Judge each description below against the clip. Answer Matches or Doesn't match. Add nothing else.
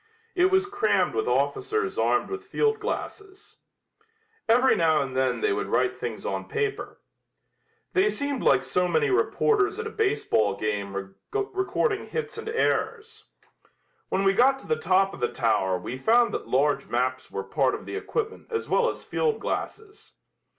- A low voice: Doesn't match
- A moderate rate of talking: Matches